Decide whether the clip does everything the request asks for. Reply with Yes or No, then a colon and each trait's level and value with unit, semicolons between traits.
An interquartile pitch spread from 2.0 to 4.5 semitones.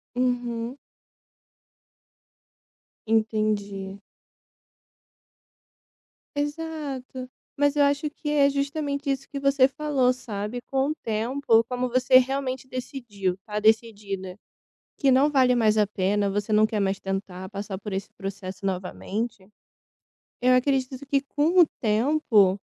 No: average, 5.1 semitones